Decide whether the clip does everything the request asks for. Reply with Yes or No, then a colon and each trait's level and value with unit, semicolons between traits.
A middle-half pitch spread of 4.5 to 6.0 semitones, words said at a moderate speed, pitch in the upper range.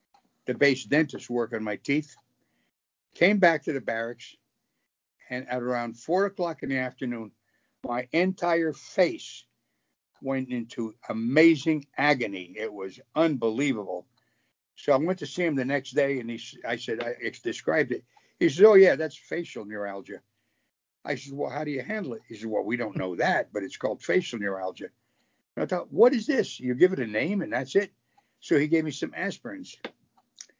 No: wide, 5.5 semitones; average, 180 wpm; low, 135 Hz